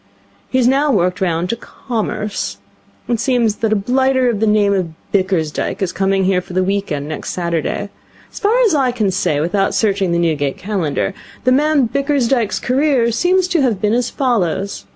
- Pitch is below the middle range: No, high, 210 Hz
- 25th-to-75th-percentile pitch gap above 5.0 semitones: Yes, wide, 5.5 semitones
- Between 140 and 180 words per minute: No, average, 190 wpm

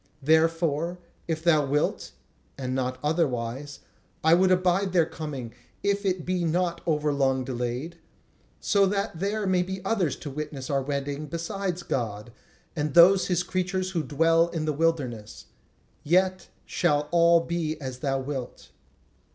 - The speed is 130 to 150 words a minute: Yes, average, 145 wpm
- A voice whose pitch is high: No, medium, 160 Hz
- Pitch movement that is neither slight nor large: Yes, average, 4.3 semitones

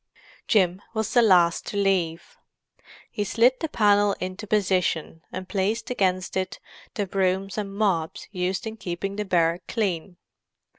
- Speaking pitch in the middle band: No, high, 195 Hz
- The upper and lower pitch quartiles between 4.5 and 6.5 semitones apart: No, narrow, 2.4 semitones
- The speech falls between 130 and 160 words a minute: Yes, average, 145 wpm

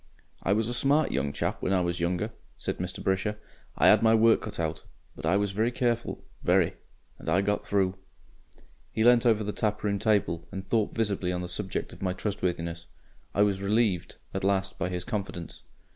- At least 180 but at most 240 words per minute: Yes, average, 195 wpm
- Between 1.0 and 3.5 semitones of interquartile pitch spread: Yes, average, 3.2 semitones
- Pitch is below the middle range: Yes, low, 100 Hz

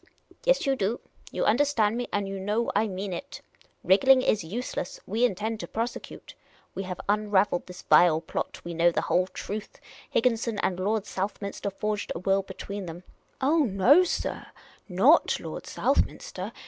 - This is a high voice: Yes, high, 205 Hz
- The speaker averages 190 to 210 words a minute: No, average, 175 wpm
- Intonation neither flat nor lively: Yes, average, 3.8 semitones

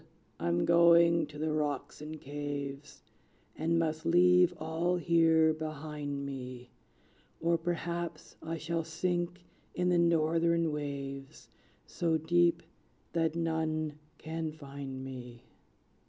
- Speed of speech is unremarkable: No, slow, 110 wpm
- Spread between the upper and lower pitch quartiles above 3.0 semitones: No, average, 2.7 semitones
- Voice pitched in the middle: Yes, medium, 160 Hz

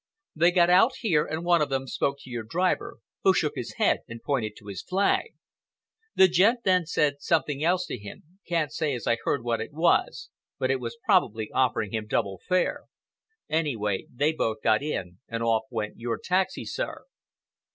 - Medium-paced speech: Yes, average, 185 wpm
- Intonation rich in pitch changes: Yes, wide, 7.3 semitones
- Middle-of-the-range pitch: Yes, medium, 145 Hz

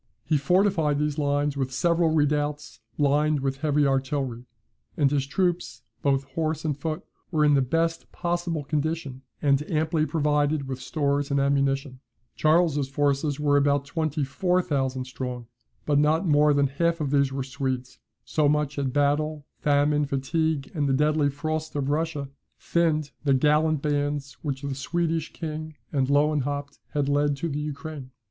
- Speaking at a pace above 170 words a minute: No, average, 160 wpm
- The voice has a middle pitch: Yes, medium, 145 Hz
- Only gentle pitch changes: Yes, narrow, 2.0 semitones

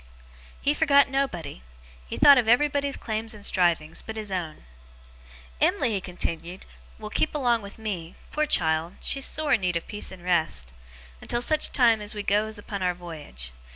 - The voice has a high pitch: Yes, high, 205 Hz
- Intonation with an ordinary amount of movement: No, wide, 5.9 semitones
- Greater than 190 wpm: No, average, 175 wpm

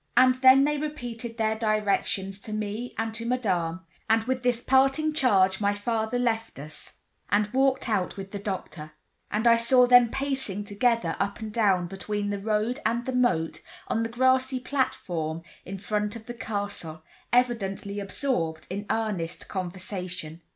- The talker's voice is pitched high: Yes, high, 220 Hz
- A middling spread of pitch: Yes, average, 4.0 semitones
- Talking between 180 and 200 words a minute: No, average, 160 wpm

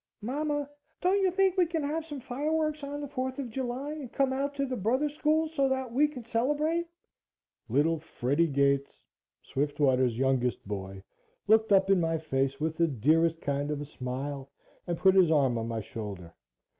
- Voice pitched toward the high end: Yes, high, 195 Hz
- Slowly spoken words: No, average, 180 wpm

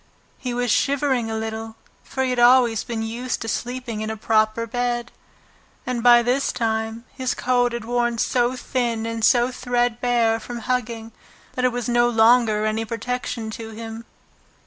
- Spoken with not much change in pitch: Yes, narrow, 1.7 semitones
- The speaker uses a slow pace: No, average, 165 wpm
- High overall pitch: Yes, high, 240 Hz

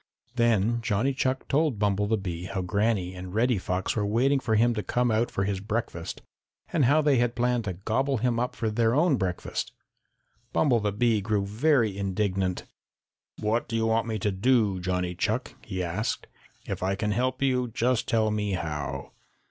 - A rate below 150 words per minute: No, average, 190 wpm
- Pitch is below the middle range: Yes, low, 110 Hz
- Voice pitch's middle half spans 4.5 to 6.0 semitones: No, average, 3.8 semitones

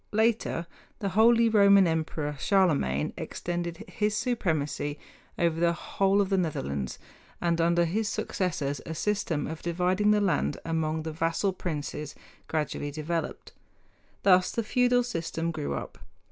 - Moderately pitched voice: Yes, medium, 170 Hz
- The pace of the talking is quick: No, slow, 135 wpm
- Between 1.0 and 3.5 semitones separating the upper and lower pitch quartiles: No, average, 4.1 semitones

